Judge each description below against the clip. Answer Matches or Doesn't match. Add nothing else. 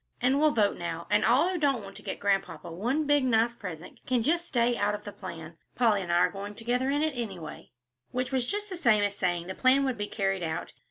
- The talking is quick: Matches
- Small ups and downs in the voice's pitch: Doesn't match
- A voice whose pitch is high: Matches